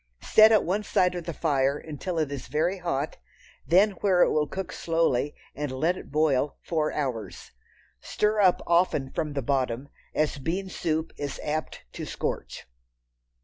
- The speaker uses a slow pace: No, average, 165 wpm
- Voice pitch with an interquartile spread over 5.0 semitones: No, average, 4.1 semitones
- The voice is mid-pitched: Yes, medium, 155 Hz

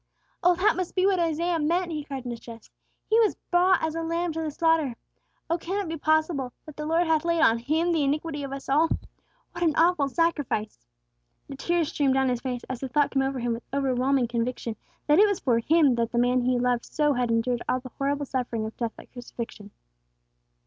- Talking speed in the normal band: No, fast, 225 wpm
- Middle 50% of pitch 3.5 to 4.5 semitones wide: No, average, 4.9 semitones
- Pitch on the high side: Yes, very high, 285 Hz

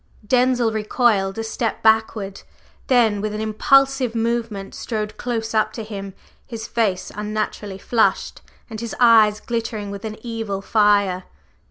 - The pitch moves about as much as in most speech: No, narrow, 2.0 semitones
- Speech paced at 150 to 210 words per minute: No, average, 140 wpm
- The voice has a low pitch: No, high, 220 Hz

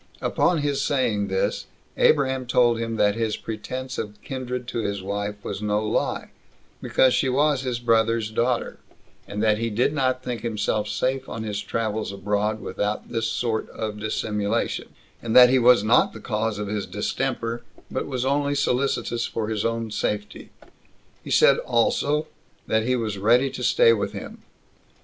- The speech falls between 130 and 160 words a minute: No, average, 170 wpm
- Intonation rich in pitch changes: No, average, 3.3 semitones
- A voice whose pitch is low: Yes, low, 115 Hz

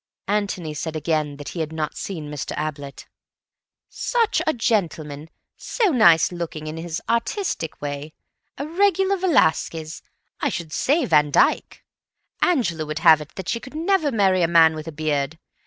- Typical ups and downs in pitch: No, wide, 7.2 semitones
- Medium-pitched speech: Yes, medium, 165 Hz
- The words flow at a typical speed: Yes, average, 155 wpm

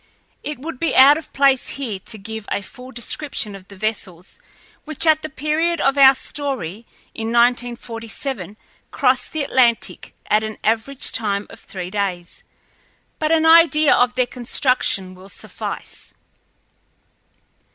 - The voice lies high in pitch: Yes, high, 245 Hz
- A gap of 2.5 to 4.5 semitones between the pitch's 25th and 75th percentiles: No, average, 5.1 semitones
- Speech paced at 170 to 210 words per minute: No, average, 140 wpm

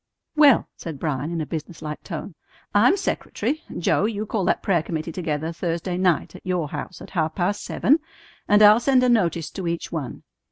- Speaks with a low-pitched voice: No, medium, 175 Hz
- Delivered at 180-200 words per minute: Yes, average, 195 wpm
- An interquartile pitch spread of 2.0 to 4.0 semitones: No, average, 4.5 semitones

